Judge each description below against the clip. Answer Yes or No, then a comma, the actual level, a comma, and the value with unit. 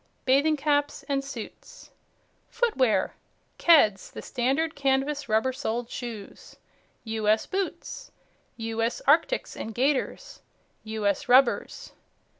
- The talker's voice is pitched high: Yes, very high, 260 Hz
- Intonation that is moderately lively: Yes, average, 4.3 semitones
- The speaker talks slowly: Yes, slow, 95 wpm